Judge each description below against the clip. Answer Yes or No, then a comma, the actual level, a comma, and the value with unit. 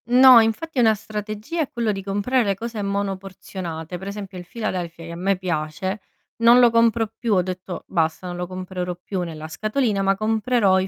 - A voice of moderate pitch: No, high, 195 Hz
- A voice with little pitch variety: No, average, 3.7 semitones